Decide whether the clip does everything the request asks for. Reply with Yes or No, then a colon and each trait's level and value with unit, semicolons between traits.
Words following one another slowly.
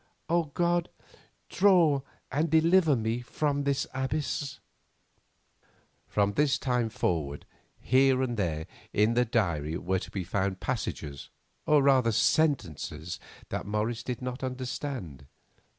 Yes: slow, 120 wpm